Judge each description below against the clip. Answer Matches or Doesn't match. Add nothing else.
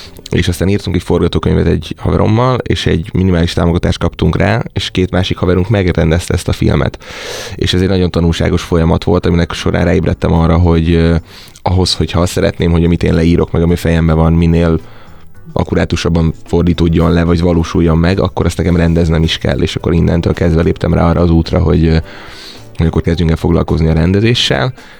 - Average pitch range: Doesn't match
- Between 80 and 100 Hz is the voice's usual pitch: Matches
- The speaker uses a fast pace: Matches